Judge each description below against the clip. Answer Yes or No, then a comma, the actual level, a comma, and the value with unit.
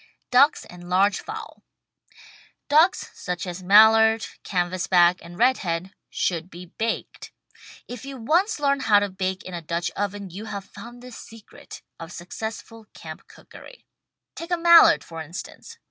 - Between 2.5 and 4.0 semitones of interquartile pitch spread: No, wide, 5.5 semitones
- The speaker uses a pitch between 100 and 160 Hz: No, high, 205 Hz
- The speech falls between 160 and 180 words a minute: No, average, 145 wpm